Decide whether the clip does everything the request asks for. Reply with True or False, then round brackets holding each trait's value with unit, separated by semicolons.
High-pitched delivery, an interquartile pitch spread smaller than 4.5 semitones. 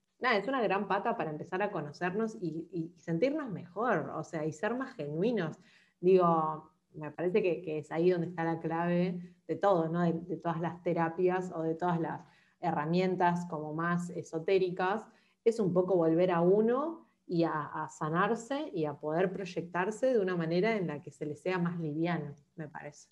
False (170 Hz; 2.7 semitones)